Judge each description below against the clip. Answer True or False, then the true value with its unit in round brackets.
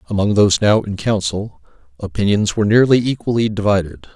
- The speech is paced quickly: False (145 wpm)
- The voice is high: False (105 Hz)